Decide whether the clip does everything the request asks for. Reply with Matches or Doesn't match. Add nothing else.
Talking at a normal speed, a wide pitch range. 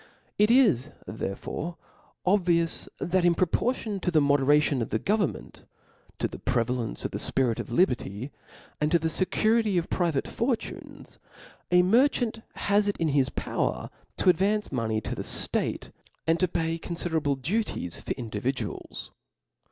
Matches